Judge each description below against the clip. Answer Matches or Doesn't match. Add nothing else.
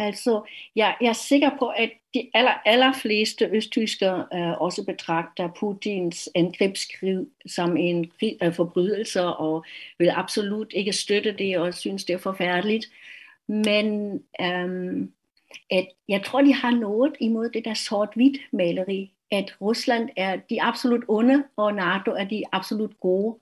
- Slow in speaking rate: Matches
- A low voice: Doesn't match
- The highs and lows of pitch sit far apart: Doesn't match